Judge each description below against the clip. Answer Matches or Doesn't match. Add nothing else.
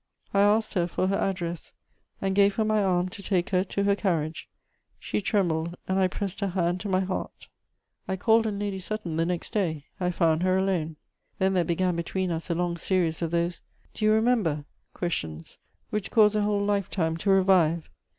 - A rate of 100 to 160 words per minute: Doesn't match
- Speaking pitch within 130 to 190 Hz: Matches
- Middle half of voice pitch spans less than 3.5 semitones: Matches